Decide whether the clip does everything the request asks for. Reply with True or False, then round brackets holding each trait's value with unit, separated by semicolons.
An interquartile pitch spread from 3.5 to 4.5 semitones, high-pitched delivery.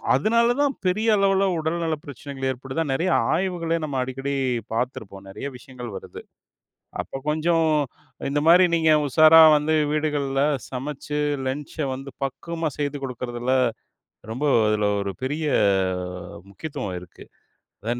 False (4.0 semitones; 145 Hz)